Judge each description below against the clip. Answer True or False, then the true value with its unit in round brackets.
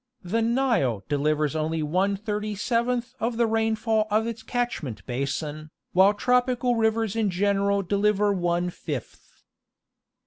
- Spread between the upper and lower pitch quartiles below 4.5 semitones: False (5.3 semitones)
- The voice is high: True (205 Hz)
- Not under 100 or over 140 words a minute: True (135 wpm)